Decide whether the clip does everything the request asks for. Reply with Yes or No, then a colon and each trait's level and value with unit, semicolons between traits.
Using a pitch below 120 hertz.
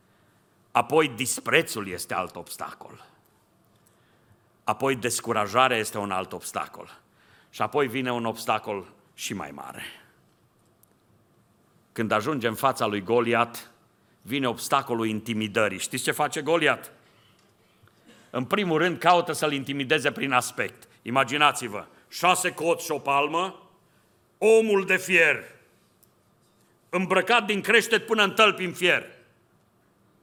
No: low, 135 Hz